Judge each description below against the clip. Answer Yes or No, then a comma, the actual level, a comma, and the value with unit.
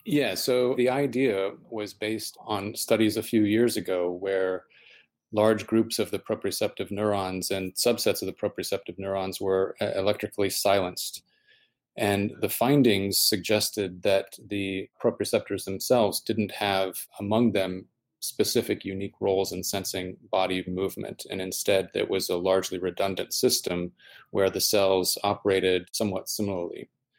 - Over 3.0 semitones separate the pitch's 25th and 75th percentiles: No, narrow, 2.4 semitones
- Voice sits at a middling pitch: No, low, 100 Hz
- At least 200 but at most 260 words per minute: No, slow, 135 wpm